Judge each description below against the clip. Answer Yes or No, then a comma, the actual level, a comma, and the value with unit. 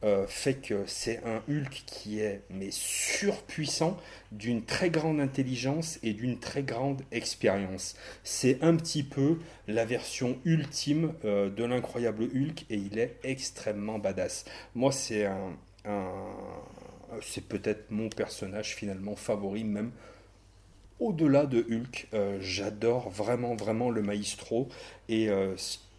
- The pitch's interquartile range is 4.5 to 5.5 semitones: Yes, average, 5.0 semitones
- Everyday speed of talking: No, slow, 120 wpm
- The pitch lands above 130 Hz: No, low, 115 Hz